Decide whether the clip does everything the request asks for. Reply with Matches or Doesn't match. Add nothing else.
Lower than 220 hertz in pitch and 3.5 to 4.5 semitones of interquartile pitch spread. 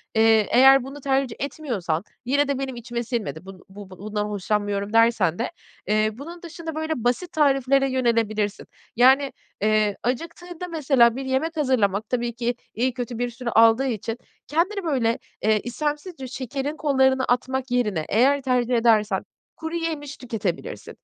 Doesn't match